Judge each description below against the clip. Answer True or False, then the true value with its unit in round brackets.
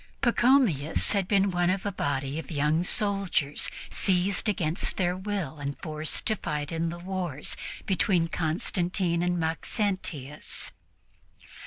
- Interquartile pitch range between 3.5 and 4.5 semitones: True (3.9 semitones)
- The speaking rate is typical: False (130 wpm)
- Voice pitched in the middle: True (175 Hz)